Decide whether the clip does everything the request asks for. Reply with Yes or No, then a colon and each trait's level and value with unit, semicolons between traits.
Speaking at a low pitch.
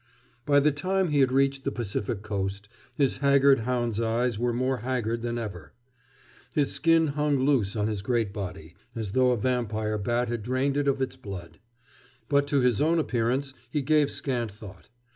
Yes: low, 125 Hz